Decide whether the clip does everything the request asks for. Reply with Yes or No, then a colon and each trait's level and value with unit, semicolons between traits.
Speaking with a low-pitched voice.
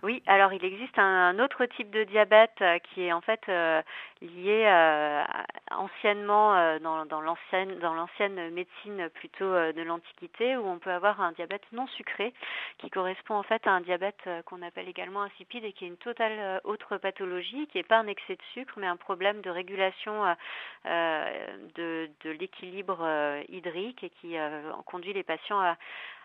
No: high, 190 Hz